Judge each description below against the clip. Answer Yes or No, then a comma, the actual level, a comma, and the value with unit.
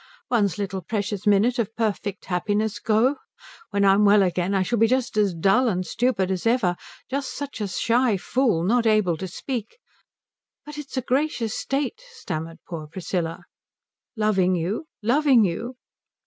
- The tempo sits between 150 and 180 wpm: Yes, average, 160 wpm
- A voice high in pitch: Yes, high, 215 Hz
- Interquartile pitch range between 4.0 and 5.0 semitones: Yes, average, 4.7 semitones